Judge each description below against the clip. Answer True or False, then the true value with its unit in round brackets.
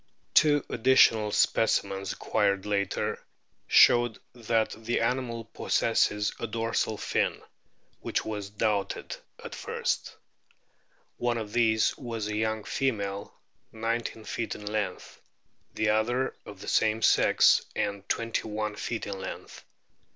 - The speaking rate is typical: False (120 wpm)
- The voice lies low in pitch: True (110 Hz)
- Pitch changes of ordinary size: False (1.9 semitones)